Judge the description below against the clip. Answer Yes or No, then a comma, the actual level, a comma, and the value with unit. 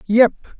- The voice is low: No, high, 225 Hz